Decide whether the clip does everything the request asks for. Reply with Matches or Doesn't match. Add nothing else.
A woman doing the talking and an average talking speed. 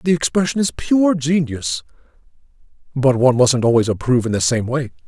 Doesn't match